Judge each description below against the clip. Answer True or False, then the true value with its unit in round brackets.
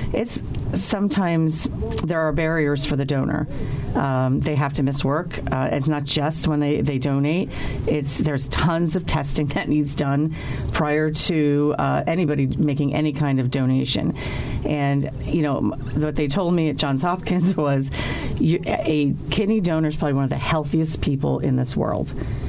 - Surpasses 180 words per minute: False (170 wpm)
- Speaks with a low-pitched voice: False (150 Hz)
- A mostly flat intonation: True (2.3 semitones)